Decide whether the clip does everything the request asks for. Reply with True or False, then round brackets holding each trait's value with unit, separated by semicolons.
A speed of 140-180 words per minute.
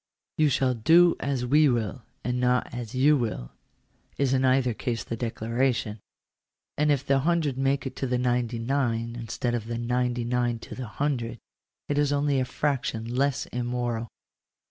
True (175 wpm)